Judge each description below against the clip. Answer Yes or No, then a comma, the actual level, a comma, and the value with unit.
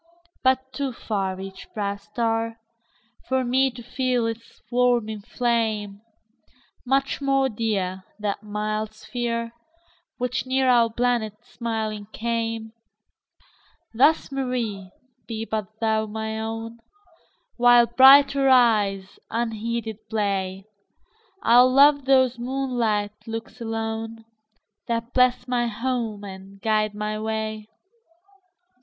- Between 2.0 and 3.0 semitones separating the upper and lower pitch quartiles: Yes, narrow, 2.5 semitones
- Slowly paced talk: Yes, slow, 85 wpm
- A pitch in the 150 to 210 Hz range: No, high, 230 Hz